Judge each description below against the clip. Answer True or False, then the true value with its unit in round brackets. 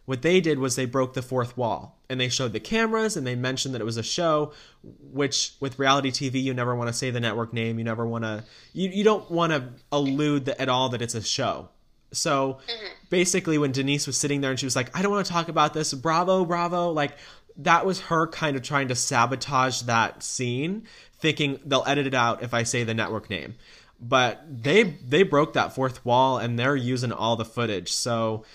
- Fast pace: True (225 wpm)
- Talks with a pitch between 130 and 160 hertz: True (135 Hz)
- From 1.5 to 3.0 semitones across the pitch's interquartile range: False (3.8 semitones)